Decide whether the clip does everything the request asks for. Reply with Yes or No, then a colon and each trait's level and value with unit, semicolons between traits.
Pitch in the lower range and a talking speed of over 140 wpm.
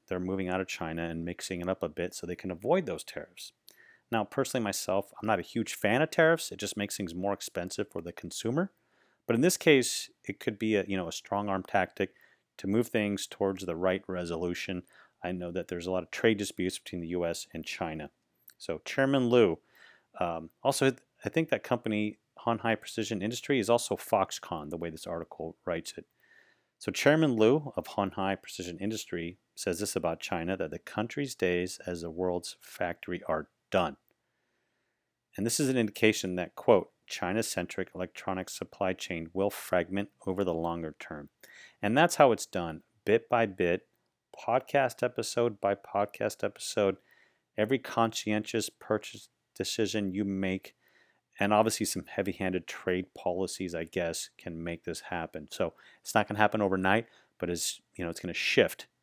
Yes: low, 100 Hz; average, 180 wpm